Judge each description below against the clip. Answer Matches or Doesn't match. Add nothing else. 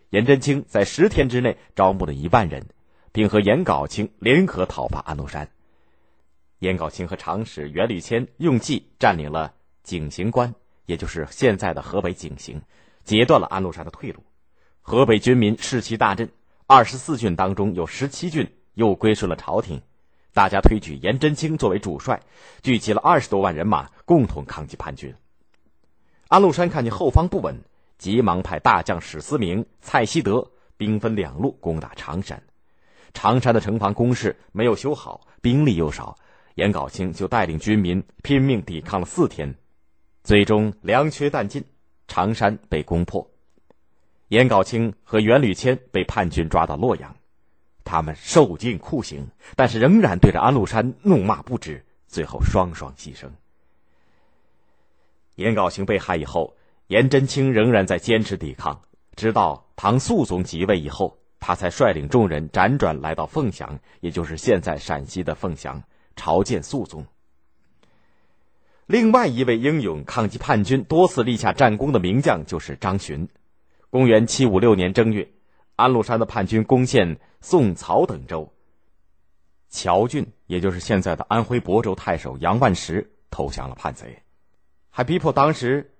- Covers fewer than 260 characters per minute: Matches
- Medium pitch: Doesn't match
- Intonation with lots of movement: Matches